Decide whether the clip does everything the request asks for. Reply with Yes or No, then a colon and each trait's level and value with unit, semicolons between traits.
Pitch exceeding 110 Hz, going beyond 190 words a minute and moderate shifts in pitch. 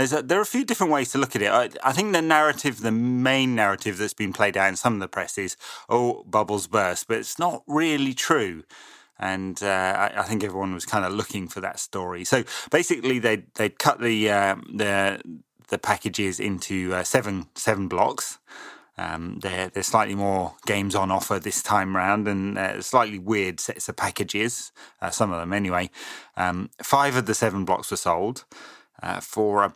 No: low, 105 Hz; average, 200 wpm; average, 4.2 semitones